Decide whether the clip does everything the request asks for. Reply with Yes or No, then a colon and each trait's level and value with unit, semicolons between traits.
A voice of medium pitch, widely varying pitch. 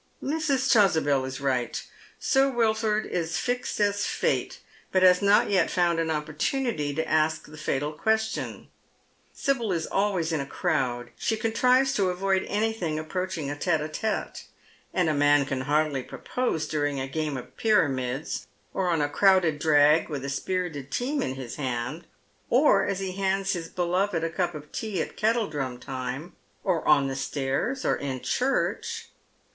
Yes: medium, 165 Hz; wide, 6.0 semitones